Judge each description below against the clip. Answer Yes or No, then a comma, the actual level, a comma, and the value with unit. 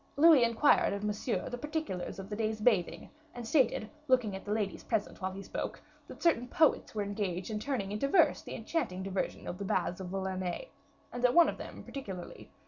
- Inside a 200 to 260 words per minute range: Yes, fast, 205 wpm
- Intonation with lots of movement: No, average, 4.5 semitones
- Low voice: No, high, 215 Hz